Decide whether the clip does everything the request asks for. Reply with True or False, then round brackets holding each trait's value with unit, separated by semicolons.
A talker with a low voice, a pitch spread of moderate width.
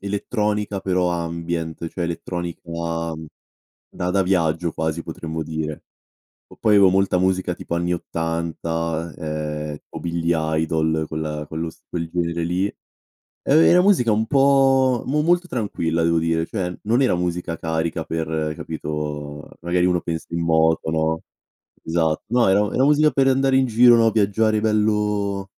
True (85 Hz; 4.5 semitones)